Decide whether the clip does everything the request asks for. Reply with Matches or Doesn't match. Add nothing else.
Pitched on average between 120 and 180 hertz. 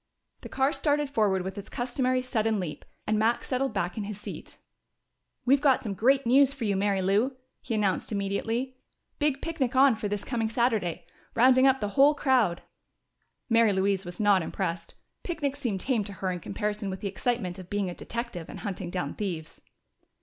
Doesn't match